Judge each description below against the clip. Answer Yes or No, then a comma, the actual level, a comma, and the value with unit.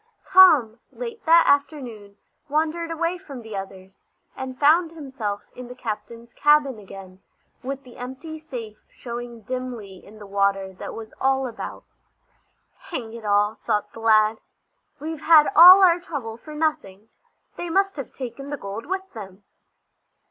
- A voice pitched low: No, very high, 250 Hz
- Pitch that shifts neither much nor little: No, wide, 6.4 semitones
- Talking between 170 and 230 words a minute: No, average, 150 wpm